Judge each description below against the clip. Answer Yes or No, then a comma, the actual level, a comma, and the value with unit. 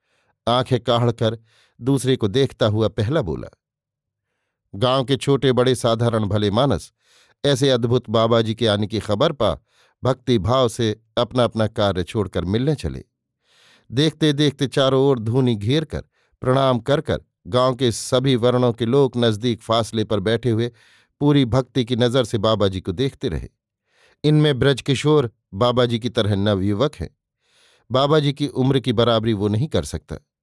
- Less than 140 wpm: No, average, 160 wpm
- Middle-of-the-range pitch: No, low, 120 Hz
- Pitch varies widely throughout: No, average, 3.2 semitones